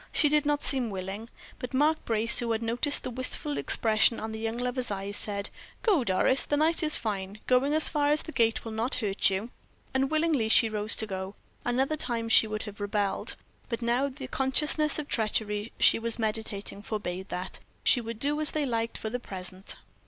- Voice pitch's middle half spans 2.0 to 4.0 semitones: No, average, 4.4 semitones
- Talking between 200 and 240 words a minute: Yes, fast, 205 wpm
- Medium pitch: No, high, 230 Hz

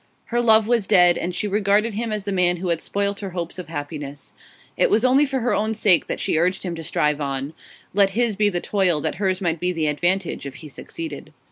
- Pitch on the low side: No, high, 190 Hz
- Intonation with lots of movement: No, average, 4.2 semitones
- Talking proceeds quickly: Yes, fast, 240 wpm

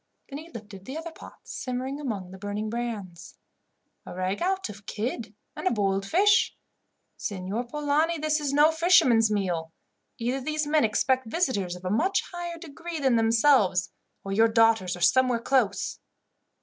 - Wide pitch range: Yes, wide, 6.8 semitones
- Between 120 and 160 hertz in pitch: No, high, 235 Hz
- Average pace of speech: Yes, average, 160 wpm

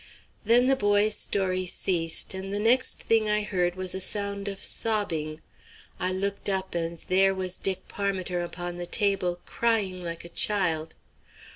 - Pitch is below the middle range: No, high, 190 Hz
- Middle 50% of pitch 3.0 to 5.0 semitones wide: No, narrow, 2.6 semitones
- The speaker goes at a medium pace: Yes, average, 160 wpm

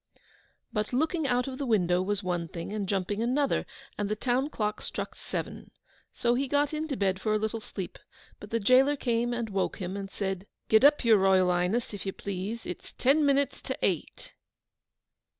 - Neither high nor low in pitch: No, high, 215 Hz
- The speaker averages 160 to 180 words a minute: No, average, 190 wpm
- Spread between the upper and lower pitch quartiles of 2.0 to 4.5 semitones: No, average, 4.9 semitones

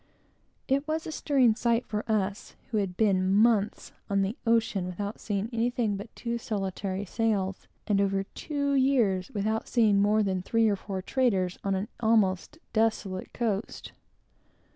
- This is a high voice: Yes, high, 210 Hz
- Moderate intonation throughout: Yes, average, 3.0 semitones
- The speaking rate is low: No, average, 160 wpm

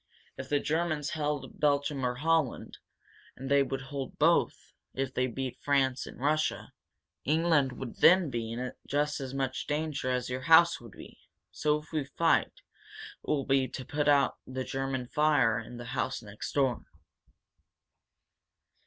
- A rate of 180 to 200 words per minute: No, average, 160 wpm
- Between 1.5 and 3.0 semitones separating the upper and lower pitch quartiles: Yes, narrow, 2.6 semitones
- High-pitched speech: No, low, 135 Hz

